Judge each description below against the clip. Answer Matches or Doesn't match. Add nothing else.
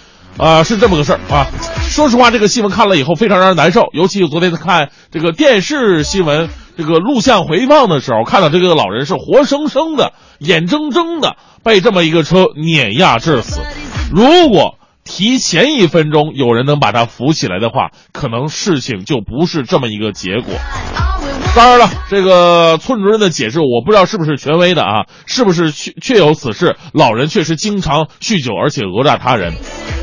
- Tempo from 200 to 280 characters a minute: Doesn't match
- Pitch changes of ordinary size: Doesn't match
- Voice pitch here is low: Doesn't match